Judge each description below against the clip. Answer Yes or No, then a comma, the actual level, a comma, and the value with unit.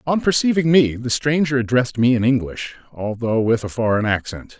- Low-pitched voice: Yes, low, 125 Hz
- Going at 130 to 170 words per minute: No, average, 185 wpm